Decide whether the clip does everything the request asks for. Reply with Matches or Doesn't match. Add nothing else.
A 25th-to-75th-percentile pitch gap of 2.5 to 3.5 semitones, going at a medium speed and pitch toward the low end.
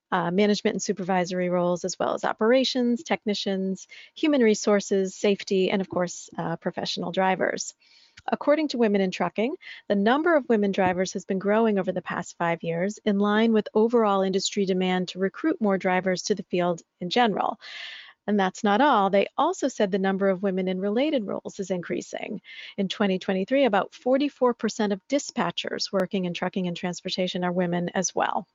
Doesn't match